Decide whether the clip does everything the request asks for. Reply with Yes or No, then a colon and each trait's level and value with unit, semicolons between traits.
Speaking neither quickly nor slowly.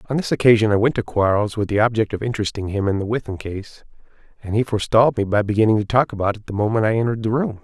No: fast, 260 wpm